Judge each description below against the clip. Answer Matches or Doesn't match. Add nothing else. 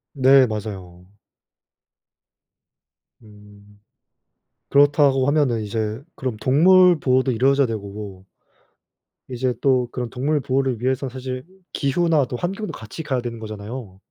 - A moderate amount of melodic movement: Matches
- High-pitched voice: Doesn't match